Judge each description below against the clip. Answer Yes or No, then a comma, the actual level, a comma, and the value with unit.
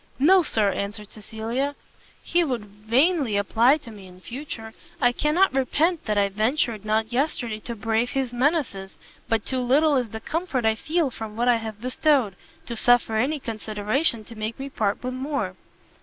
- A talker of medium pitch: No, high, 240 Hz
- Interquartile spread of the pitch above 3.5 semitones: Yes, average, 4.3 semitones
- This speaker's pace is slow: No, average, 175 wpm